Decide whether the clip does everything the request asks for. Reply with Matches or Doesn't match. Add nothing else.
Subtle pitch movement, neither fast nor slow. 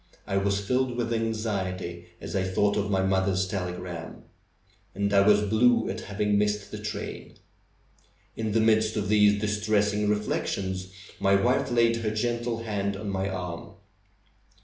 Matches